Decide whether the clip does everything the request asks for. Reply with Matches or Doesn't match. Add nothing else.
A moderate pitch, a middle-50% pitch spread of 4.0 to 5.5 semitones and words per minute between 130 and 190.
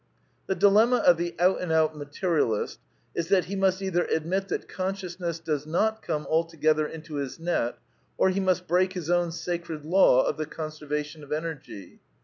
Doesn't match